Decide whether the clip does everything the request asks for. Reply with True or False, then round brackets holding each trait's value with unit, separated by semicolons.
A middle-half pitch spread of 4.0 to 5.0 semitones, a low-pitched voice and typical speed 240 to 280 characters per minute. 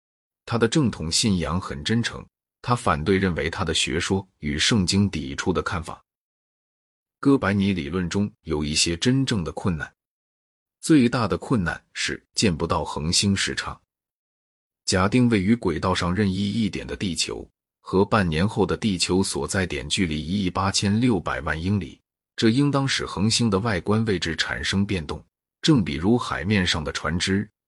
True (4.7 semitones; 95 Hz; 245 characters per minute)